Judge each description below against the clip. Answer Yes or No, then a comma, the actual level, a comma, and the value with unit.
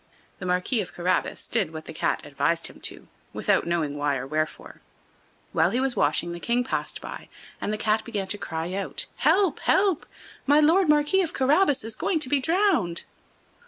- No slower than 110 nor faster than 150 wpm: No, average, 190 wpm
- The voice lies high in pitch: Yes, high, 225 Hz